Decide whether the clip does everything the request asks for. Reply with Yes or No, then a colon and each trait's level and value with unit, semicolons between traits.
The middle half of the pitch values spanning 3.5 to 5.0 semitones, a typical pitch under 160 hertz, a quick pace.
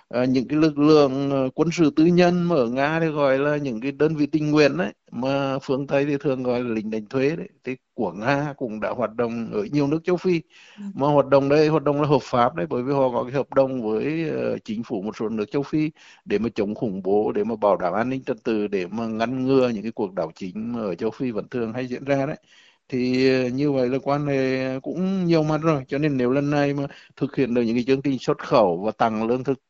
No: average, 3.0 semitones; medium, 140 Hz; fast, 265 wpm